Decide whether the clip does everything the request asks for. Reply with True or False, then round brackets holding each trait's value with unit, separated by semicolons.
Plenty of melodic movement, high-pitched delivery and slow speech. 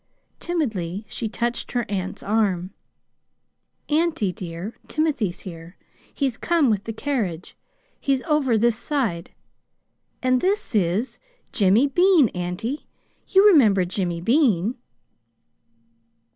True (7.2 semitones; 225 Hz; 105 wpm)